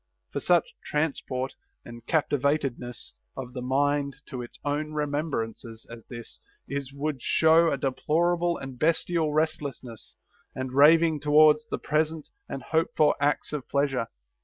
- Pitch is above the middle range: No, medium, 145 Hz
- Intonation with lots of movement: No, average, 3.0 semitones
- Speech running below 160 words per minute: Yes, slow, 135 wpm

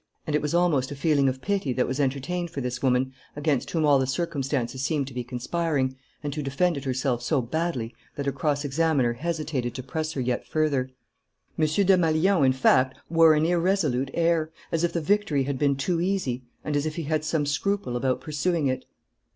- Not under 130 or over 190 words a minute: No, average, 200 wpm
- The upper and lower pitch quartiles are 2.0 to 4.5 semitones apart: Yes, average, 4.0 semitones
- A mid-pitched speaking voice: Yes, medium, 145 Hz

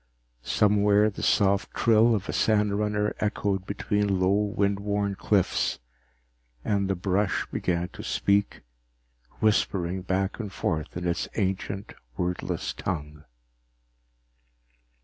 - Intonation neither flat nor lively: No, narrow, 1.9 semitones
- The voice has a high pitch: No, low, 100 Hz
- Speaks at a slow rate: Yes, slow, 110 wpm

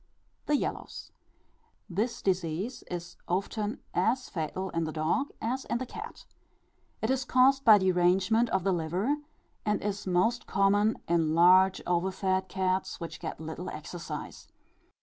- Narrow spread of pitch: No, average, 4.1 semitones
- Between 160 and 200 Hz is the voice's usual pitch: Yes, high, 190 Hz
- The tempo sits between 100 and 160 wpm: Yes, average, 140 wpm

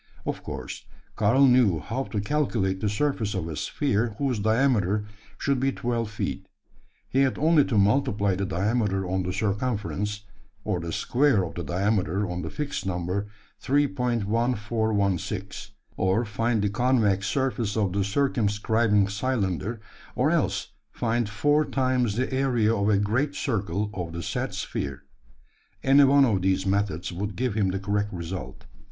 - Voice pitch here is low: Yes, low, 105 Hz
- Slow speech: No, average, 155 wpm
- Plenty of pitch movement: No, average, 4.2 semitones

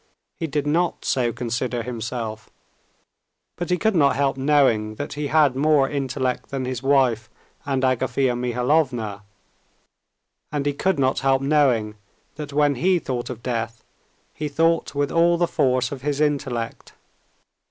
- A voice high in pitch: No, low, 135 Hz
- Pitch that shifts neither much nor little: Yes, average, 3.2 semitones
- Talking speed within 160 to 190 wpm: No, average, 150 wpm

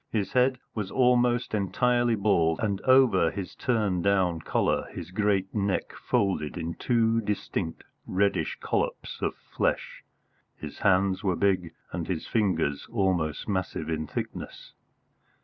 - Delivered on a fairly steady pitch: No, average, 4.0 semitones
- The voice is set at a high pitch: No, low, 100 Hz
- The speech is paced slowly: Yes, slow, 130 wpm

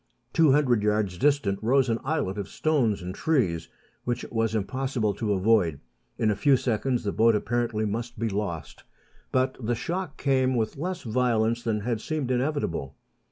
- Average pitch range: Yes, average, 4.0 semitones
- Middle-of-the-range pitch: No, low, 115 Hz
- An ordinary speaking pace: Yes, average, 170 wpm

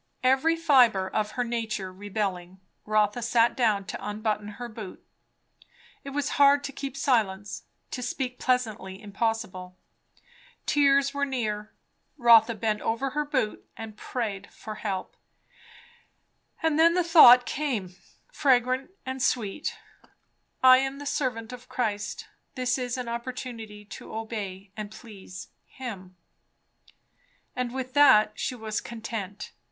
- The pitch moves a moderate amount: Yes, average, 3.8 semitones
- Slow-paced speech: Yes, slow, 130 wpm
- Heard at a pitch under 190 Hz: No, high, 235 Hz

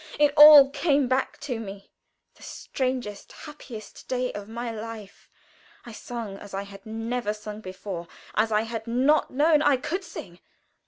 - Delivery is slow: No, average, 160 wpm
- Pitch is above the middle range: Yes, high, 230 Hz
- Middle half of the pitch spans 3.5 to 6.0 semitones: Yes, average, 4.7 semitones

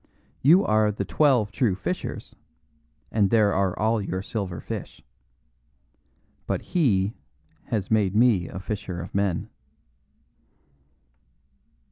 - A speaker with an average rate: No, slow, 110 wpm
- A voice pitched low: Yes, low, 105 Hz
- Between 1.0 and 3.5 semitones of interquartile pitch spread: Yes, average, 3.0 semitones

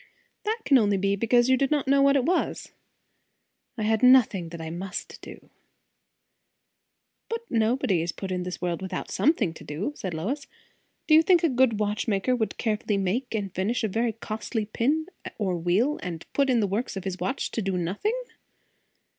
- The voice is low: No, high, 220 Hz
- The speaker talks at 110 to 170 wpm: No, average, 195 wpm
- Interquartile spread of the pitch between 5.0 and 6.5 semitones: Yes, wide, 5.6 semitones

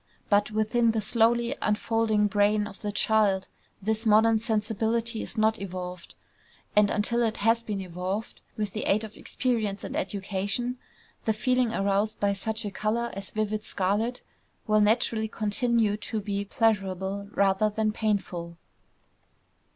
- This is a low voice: No, high, 215 Hz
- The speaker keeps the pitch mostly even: Yes, narrow, 1.9 semitones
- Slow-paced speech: No, average, 145 wpm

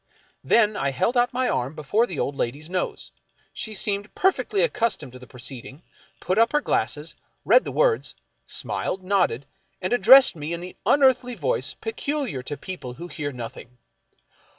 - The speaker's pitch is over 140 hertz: Yes, medium, 185 Hz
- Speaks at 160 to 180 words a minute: Yes, average, 170 wpm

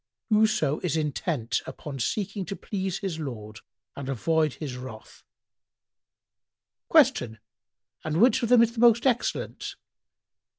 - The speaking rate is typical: No, slow, 125 wpm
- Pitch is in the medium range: Yes, medium, 160 Hz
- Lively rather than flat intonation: Yes, wide, 8.0 semitones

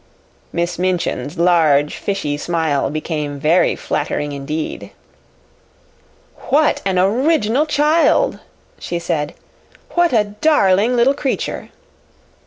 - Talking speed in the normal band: No, slow, 95 wpm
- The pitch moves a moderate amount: No, wide, 8.0 semitones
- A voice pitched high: No, medium, 180 Hz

